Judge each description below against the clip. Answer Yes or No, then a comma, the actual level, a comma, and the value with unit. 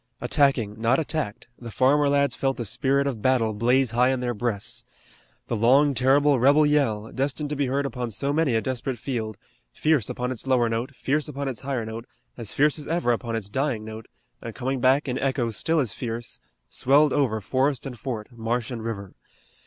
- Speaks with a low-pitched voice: Yes, low, 130 Hz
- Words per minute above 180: Yes, average, 200 wpm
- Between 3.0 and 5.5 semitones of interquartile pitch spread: Yes, average, 3.4 semitones